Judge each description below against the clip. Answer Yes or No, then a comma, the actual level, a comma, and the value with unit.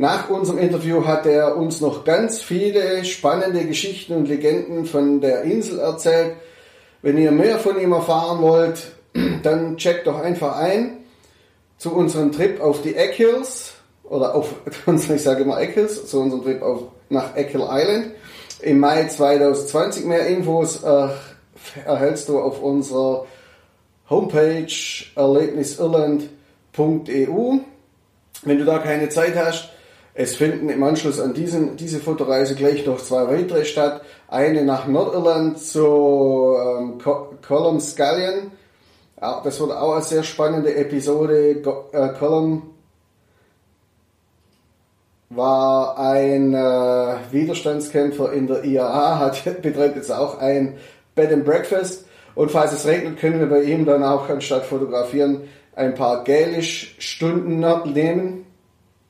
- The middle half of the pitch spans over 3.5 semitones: No, average, 3.2 semitones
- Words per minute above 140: No, average, 135 wpm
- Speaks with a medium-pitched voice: Yes, medium, 150 Hz